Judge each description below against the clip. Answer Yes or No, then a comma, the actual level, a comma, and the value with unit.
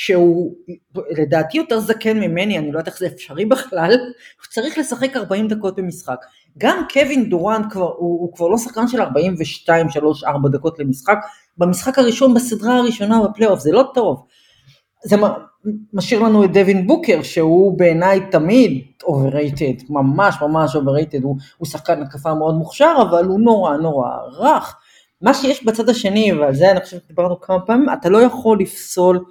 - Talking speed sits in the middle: No, fast, 165 wpm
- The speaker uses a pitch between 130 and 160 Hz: No, medium, 185 Hz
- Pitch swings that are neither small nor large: No, wide, 5.7 semitones